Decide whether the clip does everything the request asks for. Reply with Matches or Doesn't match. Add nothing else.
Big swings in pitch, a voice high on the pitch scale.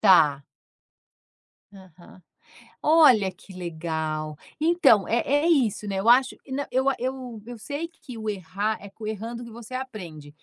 Matches